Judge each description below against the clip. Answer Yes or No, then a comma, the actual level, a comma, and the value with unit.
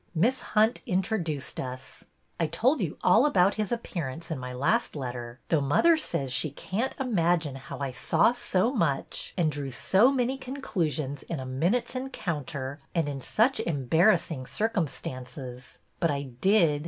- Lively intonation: Yes, wide, 8.1 semitones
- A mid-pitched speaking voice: Yes, medium, 165 Hz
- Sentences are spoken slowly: No, average, 160 wpm